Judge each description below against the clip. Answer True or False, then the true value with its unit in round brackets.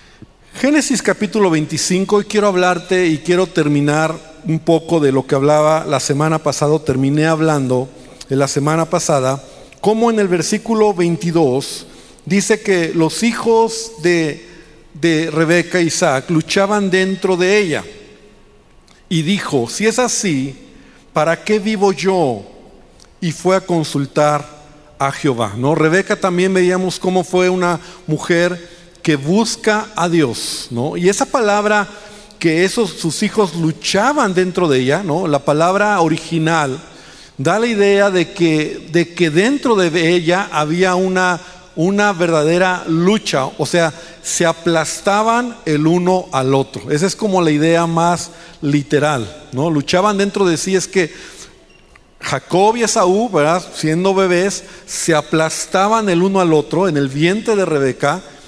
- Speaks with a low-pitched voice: False (175 Hz)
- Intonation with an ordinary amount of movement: True (3.8 semitones)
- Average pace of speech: True (140 wpm)